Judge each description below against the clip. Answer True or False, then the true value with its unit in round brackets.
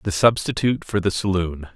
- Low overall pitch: True (95 Hz)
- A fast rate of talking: False (170 wpm)